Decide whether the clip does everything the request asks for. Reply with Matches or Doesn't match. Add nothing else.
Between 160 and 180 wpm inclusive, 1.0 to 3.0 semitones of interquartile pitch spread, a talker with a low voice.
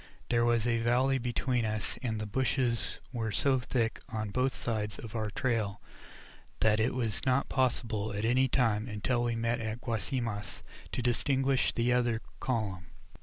Matches